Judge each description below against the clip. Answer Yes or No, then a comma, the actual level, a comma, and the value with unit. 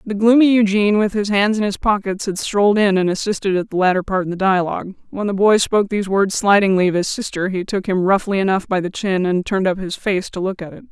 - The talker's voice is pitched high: Yes, high, 195 Hz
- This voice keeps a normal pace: No, fast, 265 wpm